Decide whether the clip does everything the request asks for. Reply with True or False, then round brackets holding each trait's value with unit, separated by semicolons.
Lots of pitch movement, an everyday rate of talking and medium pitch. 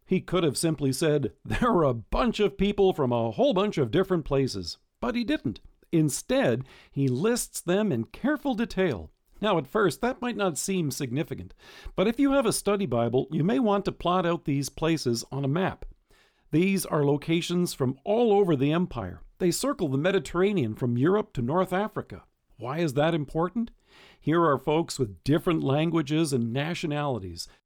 True (6.0 semitones; 180 wpm; 165 Hz)